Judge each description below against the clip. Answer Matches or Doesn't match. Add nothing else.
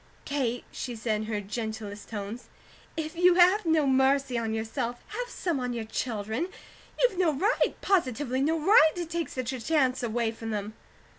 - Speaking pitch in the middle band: Doesn't match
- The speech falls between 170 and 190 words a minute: Matches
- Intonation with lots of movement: Matches